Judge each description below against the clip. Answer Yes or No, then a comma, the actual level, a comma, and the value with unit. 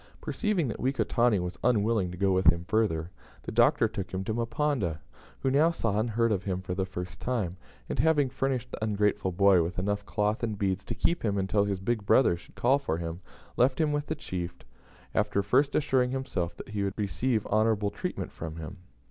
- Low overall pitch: Yes, low, 105 Hz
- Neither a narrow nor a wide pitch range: Yes, average, 5.0 semitones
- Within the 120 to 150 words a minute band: No, fast, 205 wpm